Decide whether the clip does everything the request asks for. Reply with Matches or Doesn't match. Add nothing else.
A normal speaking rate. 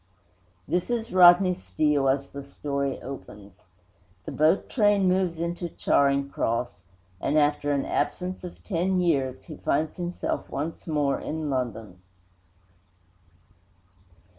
Doesn't match